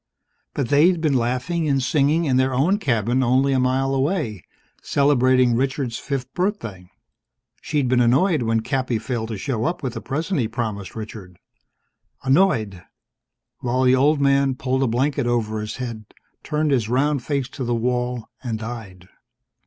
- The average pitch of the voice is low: Yes, low, 130 Hz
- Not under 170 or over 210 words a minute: No, average, 160 wpm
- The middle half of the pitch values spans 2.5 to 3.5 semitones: Yes, average, 3.2 semitones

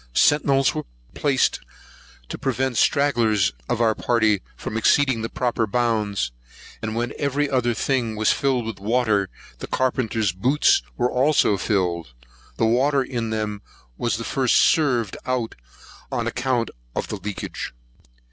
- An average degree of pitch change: Yes, average, 3.4 semitones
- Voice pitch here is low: Yes, low, 120 Hz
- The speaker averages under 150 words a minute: Yes, slow, 135 wpm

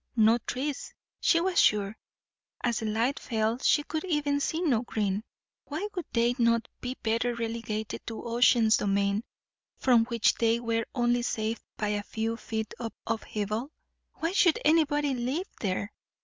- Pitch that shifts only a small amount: No, average, 3.7 semitones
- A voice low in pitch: No, high, 235 Hz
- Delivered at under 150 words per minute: No, average, 155 wpm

